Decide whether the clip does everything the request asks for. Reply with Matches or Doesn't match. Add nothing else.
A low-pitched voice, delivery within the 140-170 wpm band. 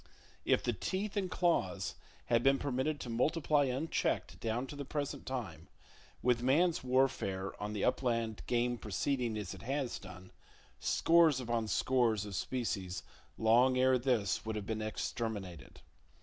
Matches